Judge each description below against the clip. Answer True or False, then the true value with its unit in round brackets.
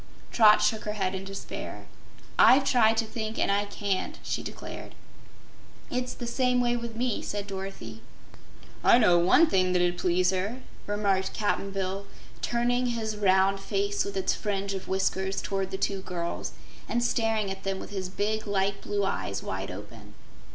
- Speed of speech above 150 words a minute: True (170 wpm)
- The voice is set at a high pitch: True (200 Hz)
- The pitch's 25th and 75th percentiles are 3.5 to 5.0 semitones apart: False (2.5 semitones)